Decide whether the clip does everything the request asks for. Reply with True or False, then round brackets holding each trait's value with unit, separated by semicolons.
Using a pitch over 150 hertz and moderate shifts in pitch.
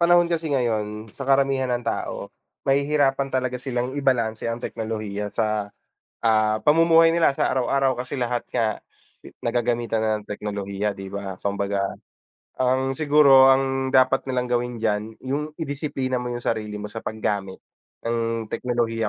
False (125 Hz; 3.8 semitones)